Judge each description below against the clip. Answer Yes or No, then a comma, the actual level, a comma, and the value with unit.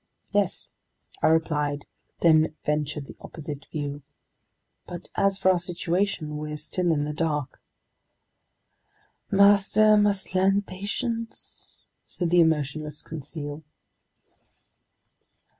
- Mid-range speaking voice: Yes, medium, 160 Hz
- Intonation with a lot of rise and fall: No, average, 4.2 semitones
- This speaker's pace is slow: Yes, slow, 100 wpm